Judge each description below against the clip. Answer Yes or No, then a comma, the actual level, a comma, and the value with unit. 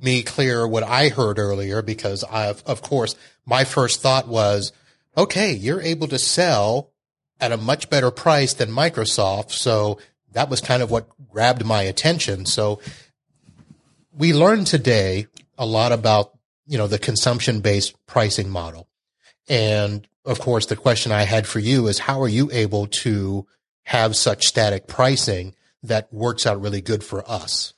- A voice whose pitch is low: Yes, low, 115 Hz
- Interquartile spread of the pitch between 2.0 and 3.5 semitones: No, average, 4.0 semitones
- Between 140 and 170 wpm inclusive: Yes, average, 160 wpm